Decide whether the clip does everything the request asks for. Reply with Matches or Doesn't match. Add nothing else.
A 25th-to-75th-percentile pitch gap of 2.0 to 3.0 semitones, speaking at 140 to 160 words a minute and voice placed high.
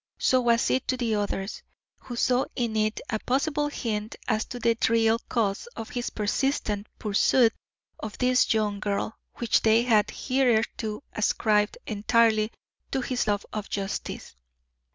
Matches